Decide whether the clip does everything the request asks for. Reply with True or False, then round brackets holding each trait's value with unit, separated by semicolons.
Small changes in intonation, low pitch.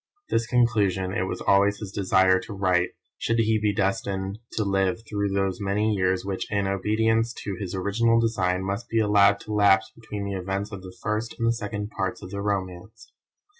True (2.3 semitones; 100 Hz)